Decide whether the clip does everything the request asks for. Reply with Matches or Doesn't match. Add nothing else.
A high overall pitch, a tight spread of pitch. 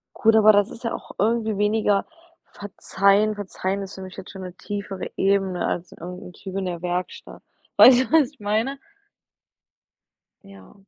Matches